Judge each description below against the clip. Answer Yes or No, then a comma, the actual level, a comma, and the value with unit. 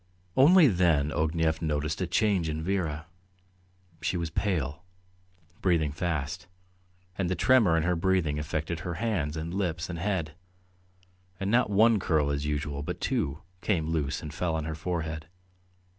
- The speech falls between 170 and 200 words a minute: No, average, 155 wpm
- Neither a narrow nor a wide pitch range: Yes, average, 3.2 semitones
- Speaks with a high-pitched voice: No, very low, 80 Hz